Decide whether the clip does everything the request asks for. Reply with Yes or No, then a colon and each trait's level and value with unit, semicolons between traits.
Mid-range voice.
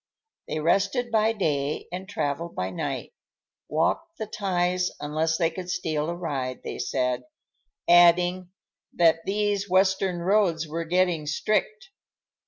Yes: medium, 175 Hz